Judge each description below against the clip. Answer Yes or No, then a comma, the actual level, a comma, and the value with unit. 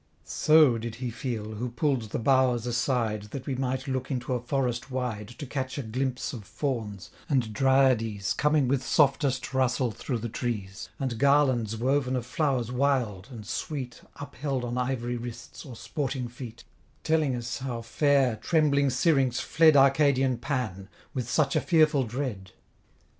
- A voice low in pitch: Yes, low, 125 Hz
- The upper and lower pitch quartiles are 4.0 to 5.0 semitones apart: No, average, 2.7 semitones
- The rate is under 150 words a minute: No, average, 160 wpm